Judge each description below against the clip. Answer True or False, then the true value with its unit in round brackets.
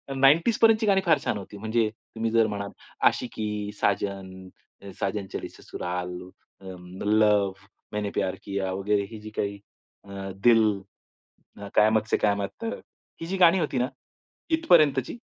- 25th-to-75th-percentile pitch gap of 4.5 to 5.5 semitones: True (5.0 semitones)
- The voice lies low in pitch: True (105 Hz)